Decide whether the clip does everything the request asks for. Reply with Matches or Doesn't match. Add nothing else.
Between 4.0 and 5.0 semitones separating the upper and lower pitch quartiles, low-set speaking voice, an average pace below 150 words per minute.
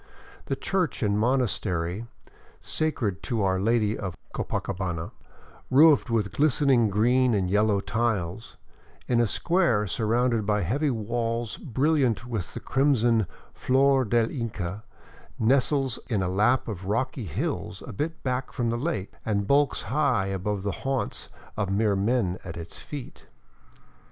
Matches